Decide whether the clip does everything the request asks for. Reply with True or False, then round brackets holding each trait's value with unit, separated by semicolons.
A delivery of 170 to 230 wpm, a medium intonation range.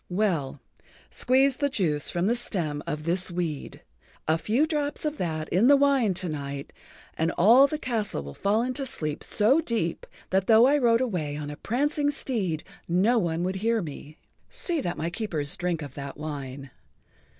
False (180 wpm; 7.9 semitones)